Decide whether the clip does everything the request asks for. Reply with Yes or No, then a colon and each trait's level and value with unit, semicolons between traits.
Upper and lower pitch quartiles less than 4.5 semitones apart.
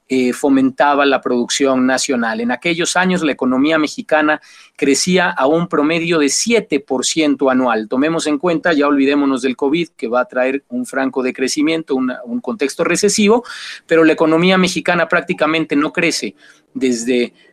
Yes: average, 4.1 semitones